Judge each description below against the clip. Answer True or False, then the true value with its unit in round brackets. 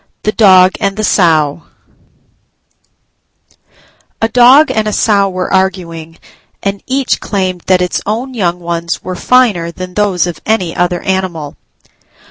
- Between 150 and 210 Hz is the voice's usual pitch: True (185 Hz)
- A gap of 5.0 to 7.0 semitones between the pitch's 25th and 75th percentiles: False (3.5 semitones)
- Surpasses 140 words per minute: False (135 wpm)